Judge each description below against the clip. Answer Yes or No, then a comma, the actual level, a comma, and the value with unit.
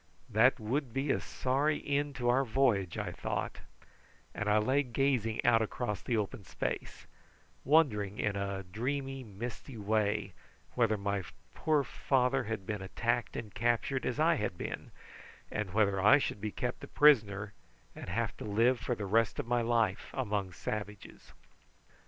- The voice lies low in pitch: Yes, low, 115 Hz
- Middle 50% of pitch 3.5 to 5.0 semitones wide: Yes, average, 4.1 semitones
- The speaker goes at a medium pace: Yes, average, 160 wpm